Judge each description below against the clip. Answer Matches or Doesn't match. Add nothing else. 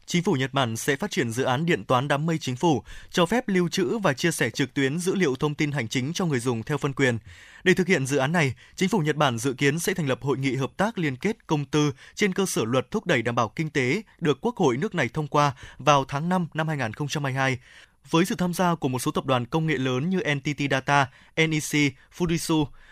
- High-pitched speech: Doesn't match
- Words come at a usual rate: Doesn't match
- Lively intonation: Doesn't match